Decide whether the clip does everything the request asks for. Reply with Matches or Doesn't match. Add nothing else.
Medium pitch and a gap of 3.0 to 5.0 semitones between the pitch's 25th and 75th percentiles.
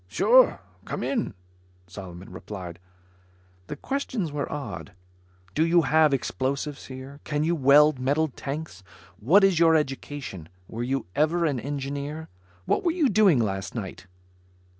Matches